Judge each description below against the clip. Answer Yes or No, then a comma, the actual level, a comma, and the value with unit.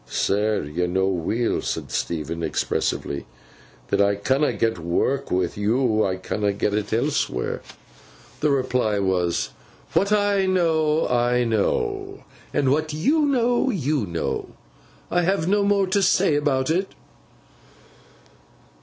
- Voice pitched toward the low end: Yes, low, 130 Hz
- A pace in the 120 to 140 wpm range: Yes, slow, 135 wpm